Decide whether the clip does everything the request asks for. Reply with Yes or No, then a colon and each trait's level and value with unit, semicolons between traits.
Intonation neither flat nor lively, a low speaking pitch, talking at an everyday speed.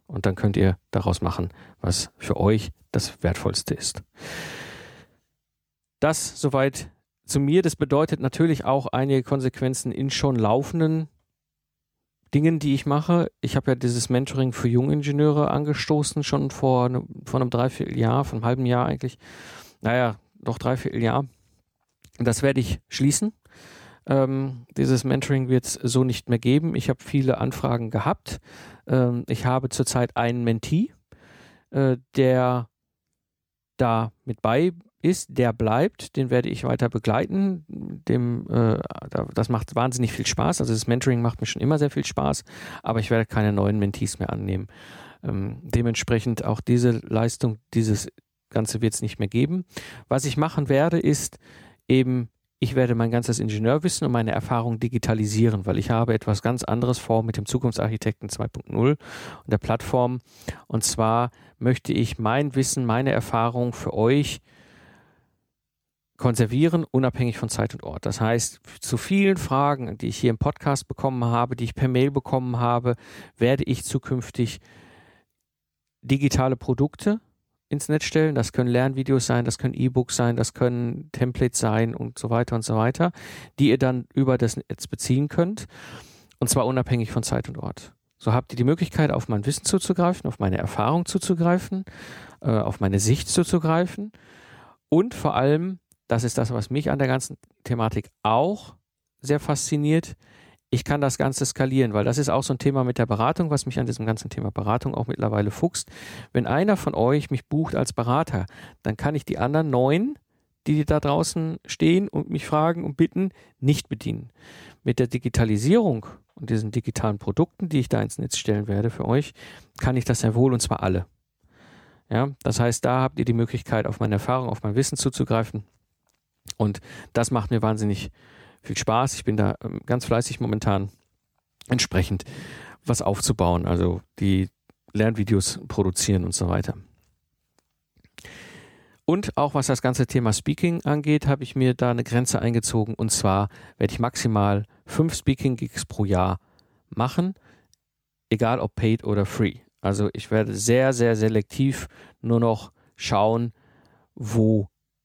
Yes: average, 3.8 semitones; low, 120 Hz; average, 160 wpm